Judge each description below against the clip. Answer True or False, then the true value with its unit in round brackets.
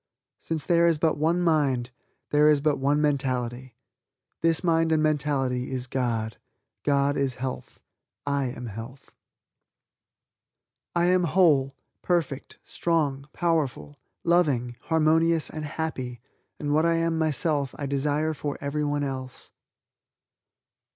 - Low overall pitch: False (145 Hz)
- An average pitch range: True (3.4 semitones)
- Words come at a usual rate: False (125 wpm)